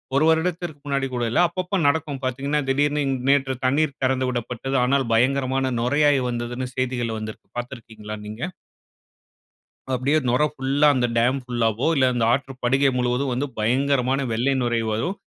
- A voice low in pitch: Yes, low, 130 Hz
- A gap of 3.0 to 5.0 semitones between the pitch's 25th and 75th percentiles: No, narrow, 2.5 semitones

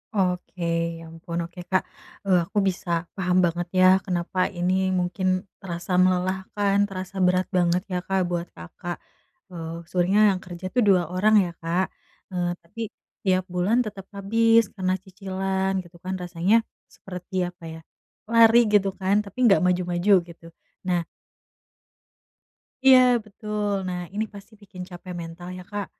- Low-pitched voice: No, medium, 185 Hz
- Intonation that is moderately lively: No, narrow, 2.0 semitones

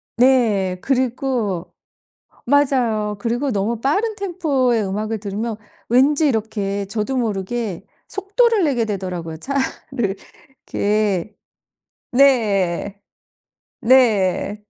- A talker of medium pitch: No, high, 225 Hz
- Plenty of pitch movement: No, average, 4.9 semitones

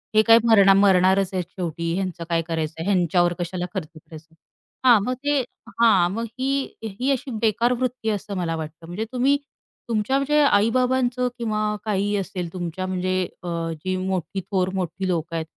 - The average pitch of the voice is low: No, high, 190 Hz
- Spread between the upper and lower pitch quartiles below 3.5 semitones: No, average, 4.7 semitones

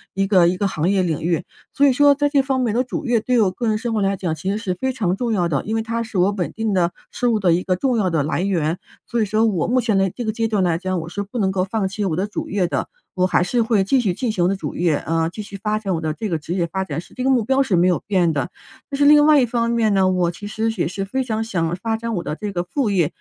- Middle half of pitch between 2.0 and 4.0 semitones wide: No, average, 4.4 semitones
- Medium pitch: No, high, 200 Hz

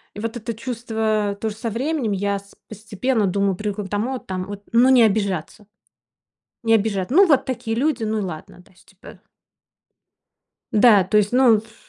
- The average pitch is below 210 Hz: No, high, 215 Hz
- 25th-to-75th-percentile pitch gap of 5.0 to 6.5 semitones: No, average, 2.8 semitones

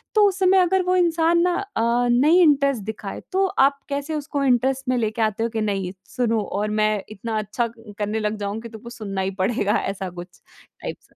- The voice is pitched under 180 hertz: No, high, 235 Hz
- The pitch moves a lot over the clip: Yes, wide, 6.2 semitones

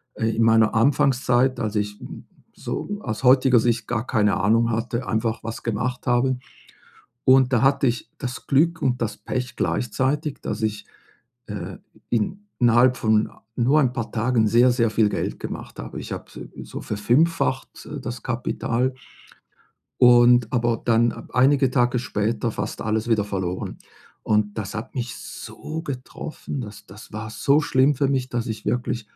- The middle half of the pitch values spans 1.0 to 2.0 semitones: No, average, 2.9 semitones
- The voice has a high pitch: No, low, 120 Hz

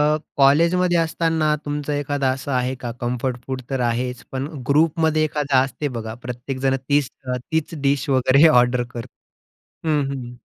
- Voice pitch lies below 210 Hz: Yes, medium, 140 Hz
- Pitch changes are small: No, average, 3.1 semitones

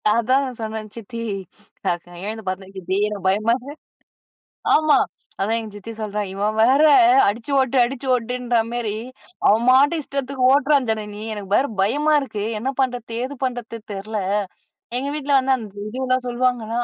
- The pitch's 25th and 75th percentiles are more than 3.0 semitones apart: Yes, average, 3.6 semitones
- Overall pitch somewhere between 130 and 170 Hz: No, high, 235 Hz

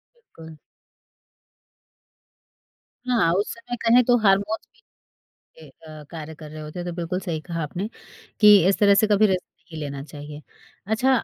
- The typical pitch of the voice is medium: Yes, medium, 180 Hz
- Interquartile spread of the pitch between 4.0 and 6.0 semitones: Yes, average, 5.3 semitones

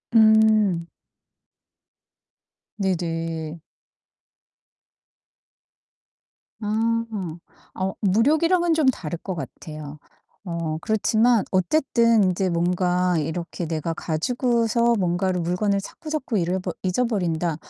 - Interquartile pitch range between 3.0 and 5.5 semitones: Yes, average, 5.2 semitones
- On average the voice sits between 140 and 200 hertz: Yes, high, 190 Hz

